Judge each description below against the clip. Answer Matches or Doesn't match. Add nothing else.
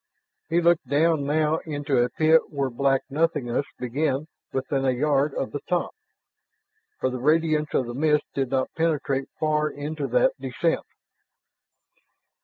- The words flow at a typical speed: Matches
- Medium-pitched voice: Matches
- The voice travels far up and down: Doesn't match